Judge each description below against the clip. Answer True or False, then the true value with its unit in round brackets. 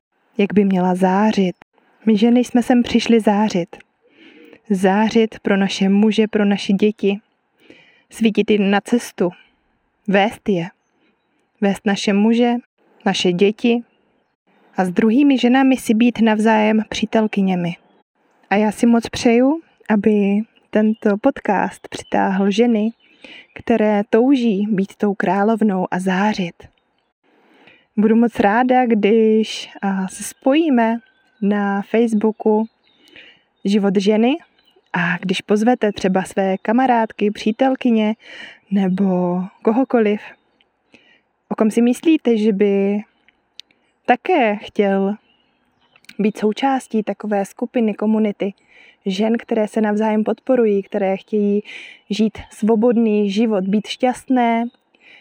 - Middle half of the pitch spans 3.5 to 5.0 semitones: False (2.8 semitones)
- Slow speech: True (105 wpm)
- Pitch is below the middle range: False (215 Hz)